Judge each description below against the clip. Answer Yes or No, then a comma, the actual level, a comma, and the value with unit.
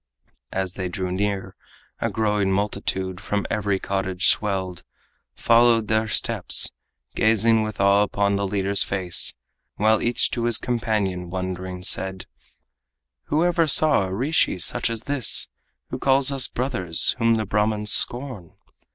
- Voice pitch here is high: No, low, 105 Hz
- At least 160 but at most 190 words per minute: No, average, 140 wpm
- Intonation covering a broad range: No, average, 3.3 semitones